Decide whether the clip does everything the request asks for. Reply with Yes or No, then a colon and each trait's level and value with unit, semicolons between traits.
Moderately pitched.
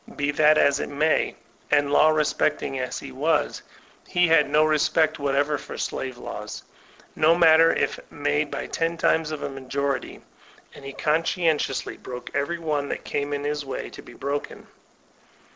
Yes: medium, 145 Hz